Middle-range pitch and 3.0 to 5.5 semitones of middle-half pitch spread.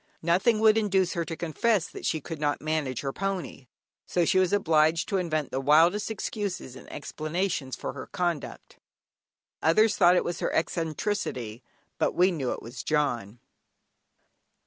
Yes: medium, 165 Hz; average, 4.4 semitones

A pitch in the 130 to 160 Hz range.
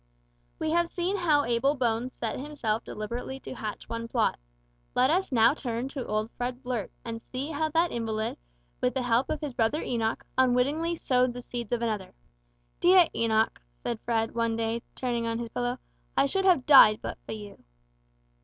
No: high, 245 Hz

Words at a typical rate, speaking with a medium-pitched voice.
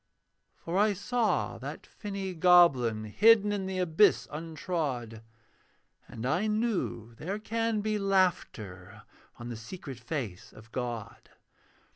No: slow, 120 wpm; medium, 170 Hz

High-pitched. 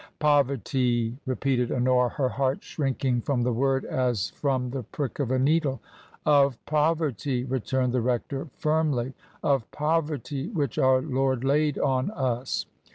No: low, 135 Hz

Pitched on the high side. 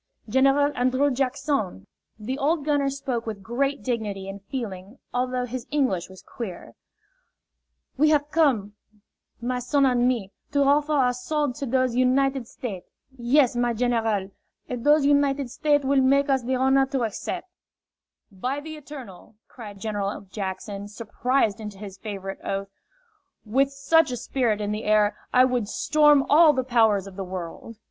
Yes: very high, 250 Hz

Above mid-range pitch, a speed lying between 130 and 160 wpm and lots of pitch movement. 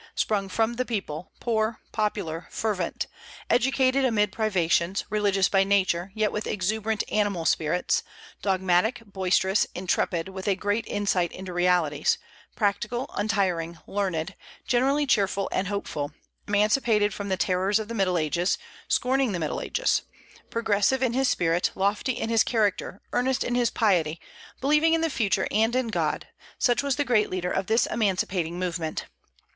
No: high, 205 Hz; average, 150 wpm; average, 3.7 semitones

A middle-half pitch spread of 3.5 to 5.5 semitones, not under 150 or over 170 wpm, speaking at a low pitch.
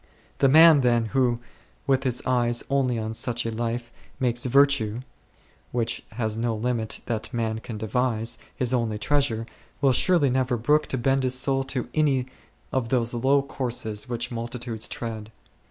No: narrow, 2.5 semitones; average, 160 wpm; low, 120 Hz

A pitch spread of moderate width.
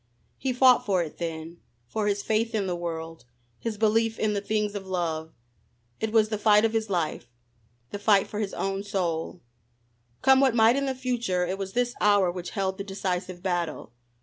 Yes: average, 3.8 semitones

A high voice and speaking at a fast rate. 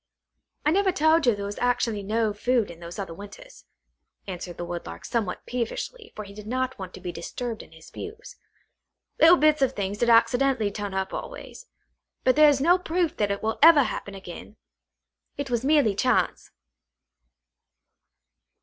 No: high, 230 Hz; average, 170 wpm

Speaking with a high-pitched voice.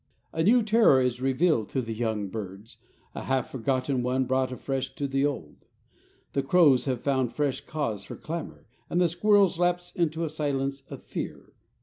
No: low, 135 Hz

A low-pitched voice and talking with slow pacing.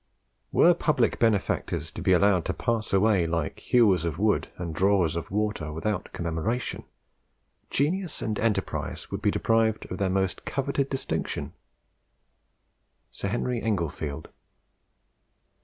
Yes: low, 100 Hz; slow, 125 wpm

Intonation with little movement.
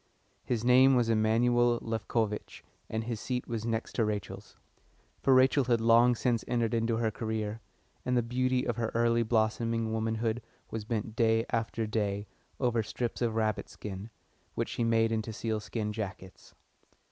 Yes: narrow, 1.5 semitones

